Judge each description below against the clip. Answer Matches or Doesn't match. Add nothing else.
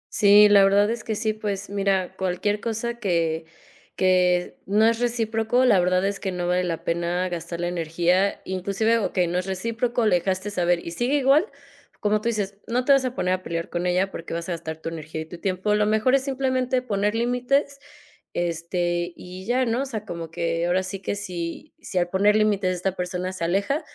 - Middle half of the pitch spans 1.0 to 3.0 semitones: Doesn't match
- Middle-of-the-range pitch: Doesn't match